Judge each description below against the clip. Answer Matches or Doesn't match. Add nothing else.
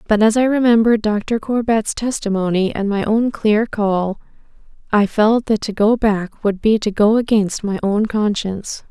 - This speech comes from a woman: Matches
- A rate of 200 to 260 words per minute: Doesn't match